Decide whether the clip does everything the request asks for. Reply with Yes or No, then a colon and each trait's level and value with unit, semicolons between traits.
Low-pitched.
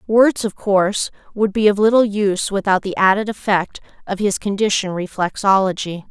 No: high, 200 Hz